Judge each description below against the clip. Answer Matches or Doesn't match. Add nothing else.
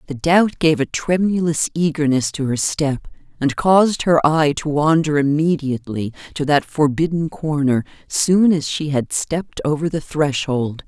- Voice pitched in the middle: Matches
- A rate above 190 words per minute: Doesn't match